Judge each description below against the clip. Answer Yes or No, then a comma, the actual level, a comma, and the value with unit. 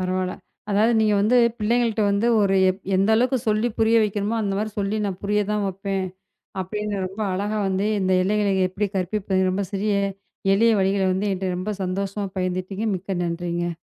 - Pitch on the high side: Yes, high, 200 Hz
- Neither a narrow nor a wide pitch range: No, narrow, 2.1 semitones